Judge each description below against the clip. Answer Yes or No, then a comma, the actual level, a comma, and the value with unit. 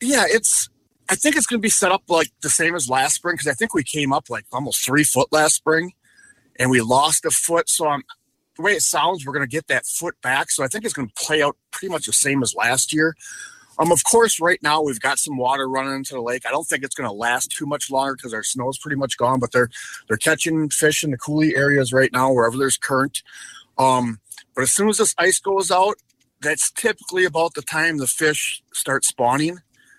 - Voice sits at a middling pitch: Yes, medium, 150 Hz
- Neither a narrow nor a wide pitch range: Yes, average, 4.0 semitones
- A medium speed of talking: No, fast, 245 wpm